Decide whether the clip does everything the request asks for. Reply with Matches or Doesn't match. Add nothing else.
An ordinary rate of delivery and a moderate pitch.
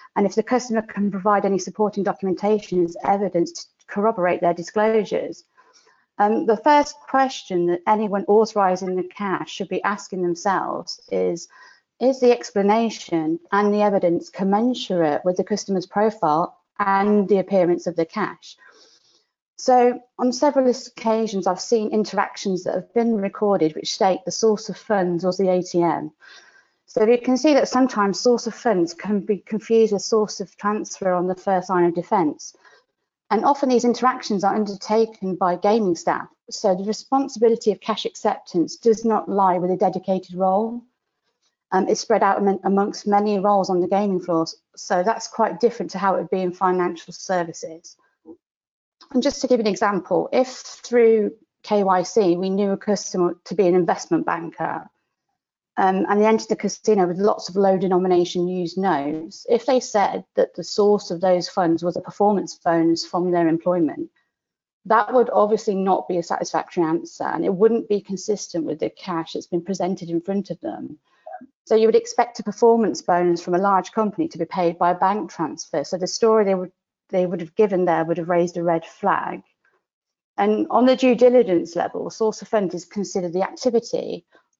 Doesn't match